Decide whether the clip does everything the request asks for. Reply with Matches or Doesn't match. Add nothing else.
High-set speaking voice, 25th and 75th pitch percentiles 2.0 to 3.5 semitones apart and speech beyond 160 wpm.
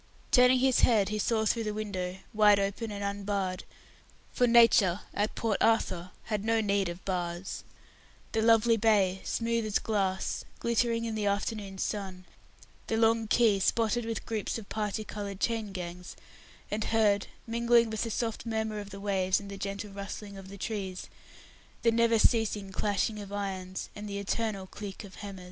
Matches